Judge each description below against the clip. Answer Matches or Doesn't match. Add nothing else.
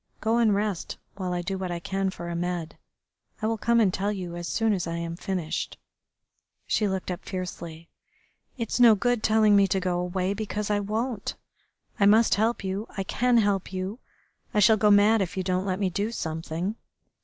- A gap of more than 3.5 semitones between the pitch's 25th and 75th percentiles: Doesn't match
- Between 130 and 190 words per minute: Doesn't match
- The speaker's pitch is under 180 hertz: Doesn't match